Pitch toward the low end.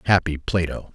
Yes: very low, 85 Hz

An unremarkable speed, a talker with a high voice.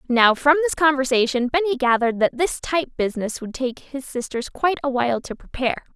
Yes: average, 190 wpm; very high, 265 Hz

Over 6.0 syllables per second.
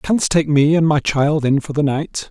No: 4.4 syllables/s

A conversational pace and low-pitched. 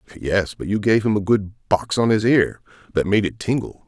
No: fast, 230 wpm; low, 105 Hz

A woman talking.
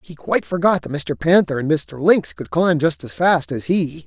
No: male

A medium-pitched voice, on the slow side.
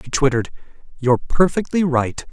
Yes: medium, 145 Hz; slow, 130 wpm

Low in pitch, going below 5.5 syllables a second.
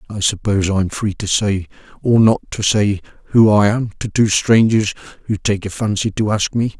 Yes: low, 105 Hz; 5.1 syllables/s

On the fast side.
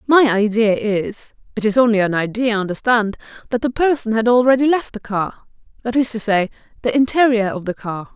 No: average, 170 wpm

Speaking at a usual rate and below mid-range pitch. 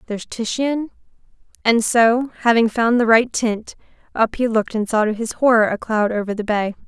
No: average, 190 wpm; high, 225 Hz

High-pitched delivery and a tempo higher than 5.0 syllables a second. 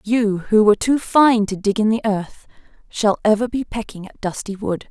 No: high, 215 Hz; 4.9 syllables/s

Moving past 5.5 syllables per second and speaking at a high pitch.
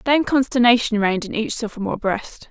Yes: 5.9 syllables/s; high, 230 Hz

